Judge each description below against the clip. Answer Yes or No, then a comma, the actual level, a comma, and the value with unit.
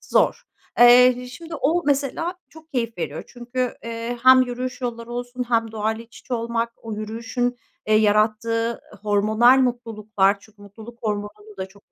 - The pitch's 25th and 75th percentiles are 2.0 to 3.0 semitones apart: Yes, narrow, 2.5 semitones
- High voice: Yes, high, 230 Hz